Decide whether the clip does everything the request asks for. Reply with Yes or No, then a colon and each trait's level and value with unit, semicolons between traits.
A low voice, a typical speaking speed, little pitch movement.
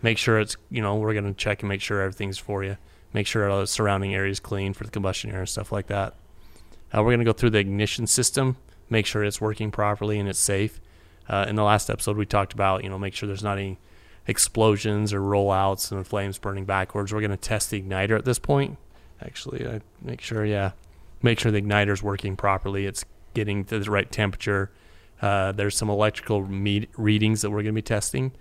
No: low, 100 Hz; fast, 220 wpm; narrow, 1.7 semitones